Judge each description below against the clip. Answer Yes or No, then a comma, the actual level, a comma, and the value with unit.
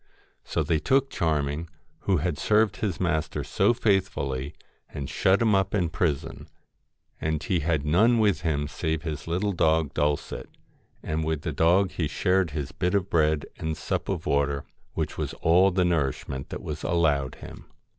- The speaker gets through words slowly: No, average, 170 wpm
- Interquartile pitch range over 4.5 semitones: No, average, 4.0 semitones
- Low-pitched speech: Yes, very low, 80 Hz